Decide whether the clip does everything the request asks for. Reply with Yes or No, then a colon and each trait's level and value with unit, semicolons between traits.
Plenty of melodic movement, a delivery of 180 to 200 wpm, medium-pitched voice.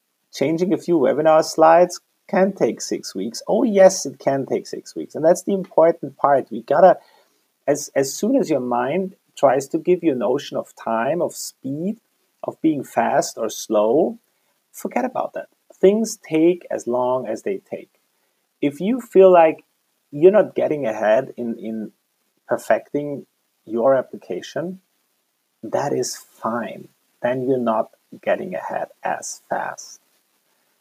No: wide, 6.4 semitones; average, 150 wpm; medium, 170 Hz